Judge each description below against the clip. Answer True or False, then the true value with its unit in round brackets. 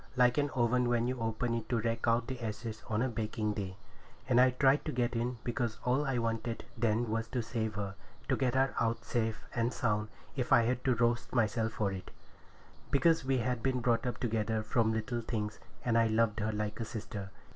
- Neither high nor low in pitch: False (115 Hz)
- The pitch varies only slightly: True (2.0 semitones)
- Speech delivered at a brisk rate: True (210 wpm)